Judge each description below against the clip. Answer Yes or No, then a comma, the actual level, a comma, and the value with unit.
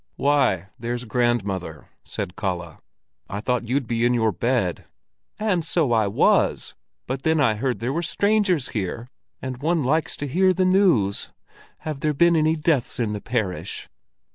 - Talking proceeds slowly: No, average, 165 wpm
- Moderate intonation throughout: No, wide, 6.4 semitones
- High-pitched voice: No, low, 125 Hz